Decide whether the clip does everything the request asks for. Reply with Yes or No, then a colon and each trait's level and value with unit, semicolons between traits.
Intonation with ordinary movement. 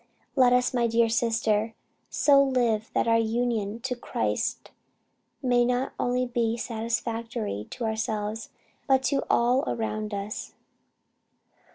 No: narrow, 1.9 semitones